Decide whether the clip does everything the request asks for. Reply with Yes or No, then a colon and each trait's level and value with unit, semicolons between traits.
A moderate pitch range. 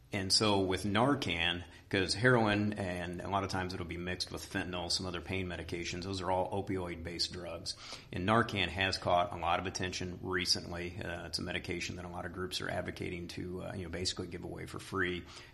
No: narrow, 2.0 semitones